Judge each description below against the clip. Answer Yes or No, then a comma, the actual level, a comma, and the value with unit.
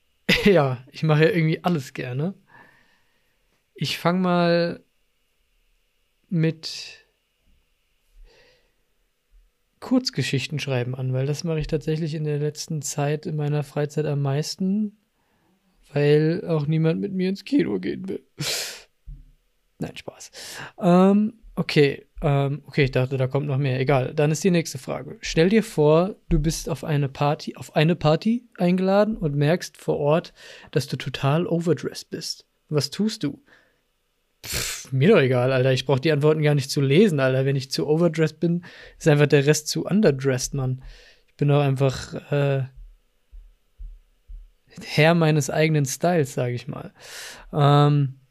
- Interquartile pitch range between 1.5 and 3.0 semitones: No, average, 3.8 semitones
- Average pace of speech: Yes, average, 145 wpm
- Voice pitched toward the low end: No, medium, 150 Hz